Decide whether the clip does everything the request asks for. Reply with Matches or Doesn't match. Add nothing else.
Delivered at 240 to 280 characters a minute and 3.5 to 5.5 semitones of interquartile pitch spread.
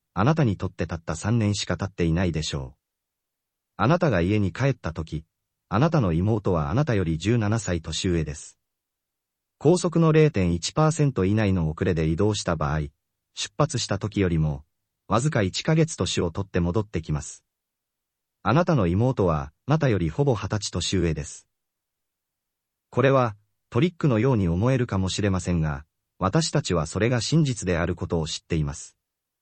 Doesn't match